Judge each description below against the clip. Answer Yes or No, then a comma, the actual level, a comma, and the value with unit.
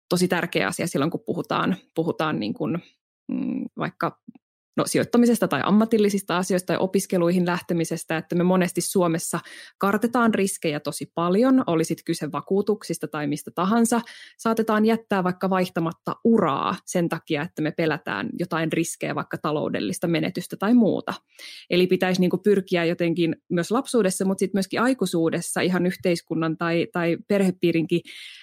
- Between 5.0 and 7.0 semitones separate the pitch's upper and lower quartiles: No, average, 3.7 semitones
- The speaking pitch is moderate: Yes, medium, 180 Hz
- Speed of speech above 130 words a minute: Yes, average, 140 wpm